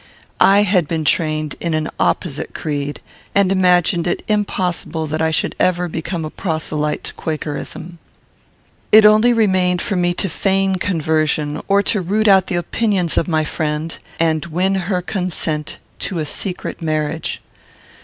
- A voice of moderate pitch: Yes, medium, 175 Hz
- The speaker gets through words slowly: No, average, 155 wpm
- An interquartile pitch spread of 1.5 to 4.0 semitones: Yes, average, 3.5 semitones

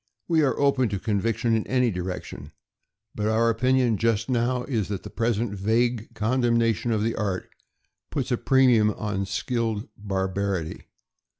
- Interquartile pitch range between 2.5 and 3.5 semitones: Yes, average, 3.1 semitones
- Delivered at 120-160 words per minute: Yes, average, 155 wpm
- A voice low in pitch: Yes, low, 115 Hz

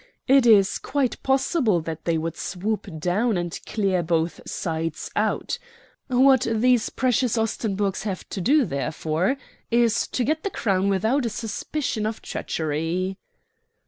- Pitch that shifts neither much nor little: No, wide, 5.9 semitones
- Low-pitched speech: No, high, 210 Hz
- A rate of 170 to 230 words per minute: No, average, 140 wpm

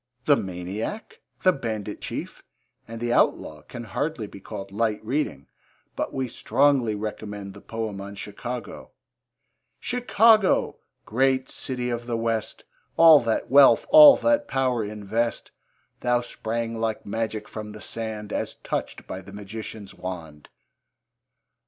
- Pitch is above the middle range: No, low, 115 Hz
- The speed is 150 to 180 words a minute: No, slow, 135 wpm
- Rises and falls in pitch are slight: No, average, 3.8 semitones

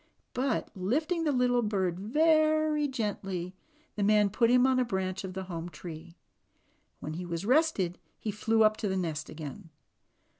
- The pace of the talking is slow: No, average, 165 wpm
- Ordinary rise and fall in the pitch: No, wide, 5.8 semitones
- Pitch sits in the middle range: No, high, 210 Hz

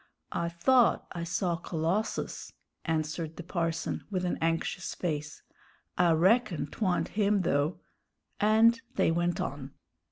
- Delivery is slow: Yes, slow, 125 wpm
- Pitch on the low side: No, medium, 170 Hz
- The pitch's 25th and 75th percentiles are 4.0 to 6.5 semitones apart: No, average, 3.4 semitones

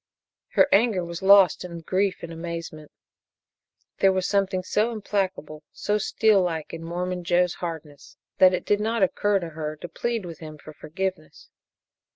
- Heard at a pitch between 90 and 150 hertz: No, medium, 180 Hz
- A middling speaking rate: Yes, average, 165 wpm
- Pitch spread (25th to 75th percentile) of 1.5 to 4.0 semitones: Yes, average, 3.1 semitones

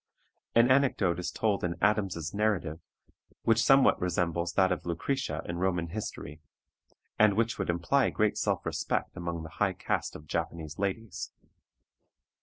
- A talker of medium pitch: No, very low, 95 Hz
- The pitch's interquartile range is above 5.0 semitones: No, average, 4.2 semitones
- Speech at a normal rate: Yes, average, 145 wpm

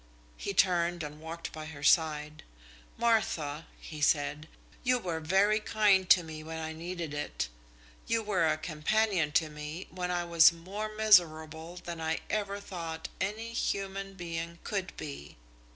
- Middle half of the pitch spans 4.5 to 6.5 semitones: No, average, 3.8 semitones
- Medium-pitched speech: Yes, medium, 170 Hz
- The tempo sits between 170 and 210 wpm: No, average, 150 wpm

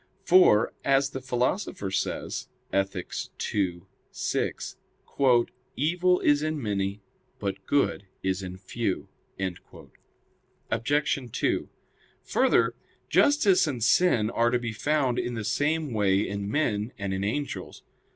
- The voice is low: Yes, low, 120 Hz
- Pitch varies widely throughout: Yes, wide, 6.6 semitones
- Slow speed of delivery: Yes, slow, 120 wpm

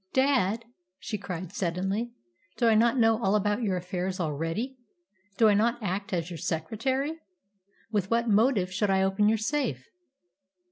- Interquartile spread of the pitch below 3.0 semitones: No, average, 3.9 semitones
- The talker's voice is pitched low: No, high, 210 Hz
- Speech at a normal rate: Yes, average, 155 wpm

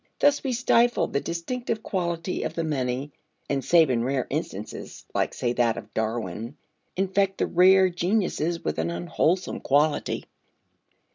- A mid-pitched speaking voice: Yes, medium, 165 Hz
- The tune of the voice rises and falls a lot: Yes, wide, 7.3 semitones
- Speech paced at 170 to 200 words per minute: No, average, 145 wpm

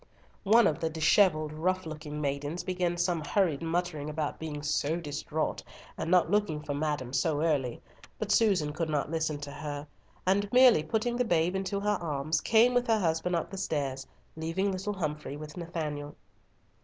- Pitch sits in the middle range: Yes, medium, 160 Hz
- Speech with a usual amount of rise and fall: Yes, average, 3.8 semitones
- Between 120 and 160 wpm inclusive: No, average, 175 wpm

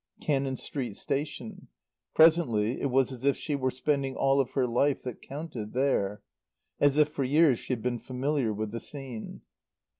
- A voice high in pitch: No, low, 135 Hz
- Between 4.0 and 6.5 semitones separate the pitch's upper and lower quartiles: No, average, 2.8 semitones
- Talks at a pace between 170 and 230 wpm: Yes, average, 175 wpm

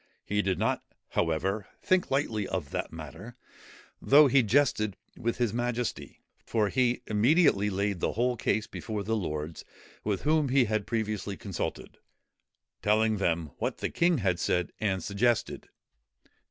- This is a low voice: Yes, low, 110 Hz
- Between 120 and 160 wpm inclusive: Yes, average, 145 wpm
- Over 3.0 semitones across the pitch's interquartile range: Yes, average, 3.8 semitones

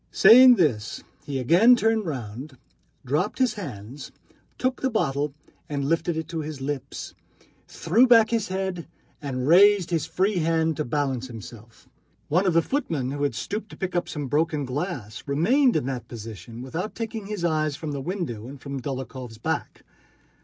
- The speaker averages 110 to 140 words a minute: No, average, 170 wpm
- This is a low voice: No, medium, 155 Hz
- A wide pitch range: Yes, wide, 6.5 semitones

